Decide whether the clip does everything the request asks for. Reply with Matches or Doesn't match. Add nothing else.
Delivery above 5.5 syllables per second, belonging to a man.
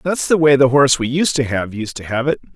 Matches